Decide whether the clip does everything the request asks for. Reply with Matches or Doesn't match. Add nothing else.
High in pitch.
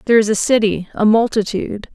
Matches